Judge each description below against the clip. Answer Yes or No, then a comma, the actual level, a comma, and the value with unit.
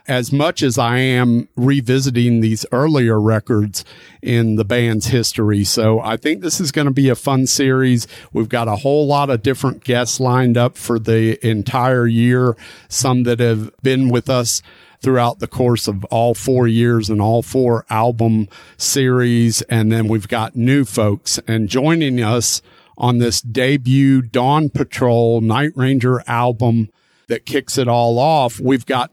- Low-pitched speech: Yes, low, 120 Hz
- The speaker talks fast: No, average, 165 wpm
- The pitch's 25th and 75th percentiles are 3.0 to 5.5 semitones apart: No, narrow, 2.6 semitones